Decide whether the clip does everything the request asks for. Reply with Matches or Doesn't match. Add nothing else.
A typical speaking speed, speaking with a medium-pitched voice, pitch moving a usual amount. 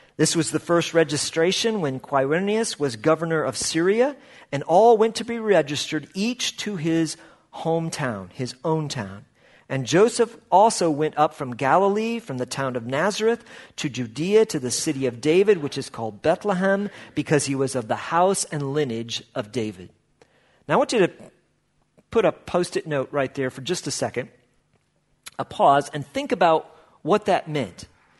Doesn't match